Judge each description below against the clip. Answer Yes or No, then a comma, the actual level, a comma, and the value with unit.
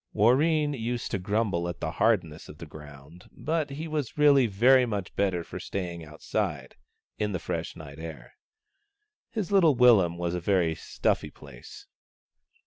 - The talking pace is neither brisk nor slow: Yes, average, 160 wpm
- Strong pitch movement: Yes, wide, 7.6 semitones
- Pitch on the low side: Yes, low, 100 Hz